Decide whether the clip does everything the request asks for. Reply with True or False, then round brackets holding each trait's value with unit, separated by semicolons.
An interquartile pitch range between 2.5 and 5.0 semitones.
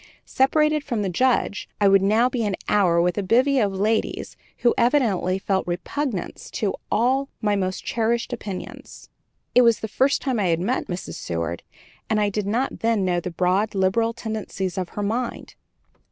True (4.1 semitones)